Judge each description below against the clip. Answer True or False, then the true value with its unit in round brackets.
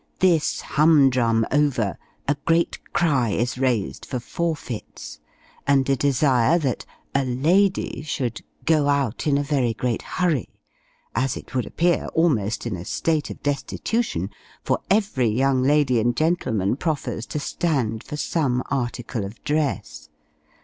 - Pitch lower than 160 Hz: True (135 Hz)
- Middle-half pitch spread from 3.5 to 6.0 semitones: True (4.3 semitones)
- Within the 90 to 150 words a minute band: True (140 wpm)